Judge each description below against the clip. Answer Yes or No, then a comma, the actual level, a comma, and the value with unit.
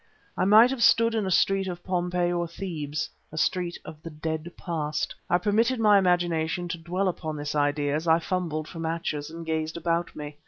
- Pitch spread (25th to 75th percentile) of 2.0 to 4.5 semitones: Yes, average, 2.7 semitones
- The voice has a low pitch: No, medium, 170 Hz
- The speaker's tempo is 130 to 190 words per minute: No, average, 200 wpm